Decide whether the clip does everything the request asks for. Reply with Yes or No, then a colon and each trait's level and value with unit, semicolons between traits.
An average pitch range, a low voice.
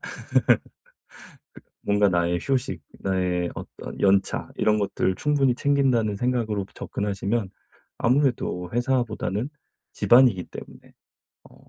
Yes: average, 4.7 semitones; low, 105 Hz